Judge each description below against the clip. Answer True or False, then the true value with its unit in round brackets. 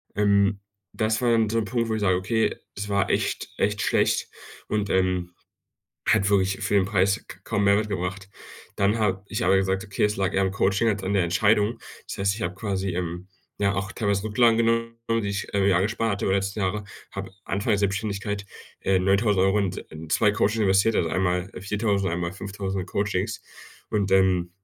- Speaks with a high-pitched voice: False (100 Hz)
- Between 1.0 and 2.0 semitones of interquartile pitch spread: True (1.7 semitones)